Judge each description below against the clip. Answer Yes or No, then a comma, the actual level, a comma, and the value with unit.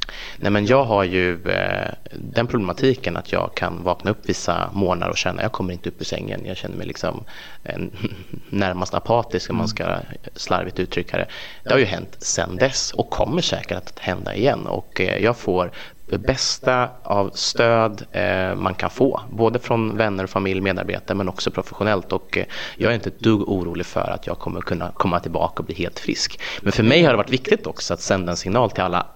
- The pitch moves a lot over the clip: No, average, 3.8 semitones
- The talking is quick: Yes, fast, 200 wpm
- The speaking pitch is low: Yes, low, 100 Hz